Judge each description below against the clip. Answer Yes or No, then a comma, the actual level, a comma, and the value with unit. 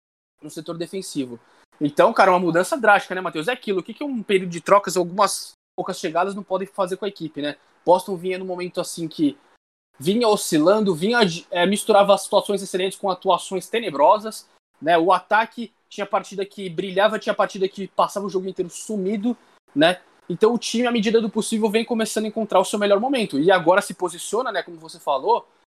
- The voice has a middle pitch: No, high, 195 Hz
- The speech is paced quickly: Yes, fast, 195 wpm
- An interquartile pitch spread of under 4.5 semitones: Yes, average, 3.3 semitones